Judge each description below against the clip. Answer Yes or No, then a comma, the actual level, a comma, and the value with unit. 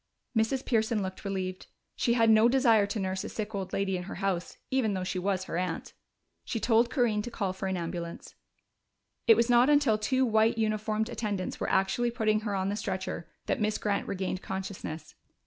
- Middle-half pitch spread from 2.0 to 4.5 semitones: Yes, average, 3.2 semitones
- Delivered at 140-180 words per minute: No, average, 200 wpm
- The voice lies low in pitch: No, high, 210 Hz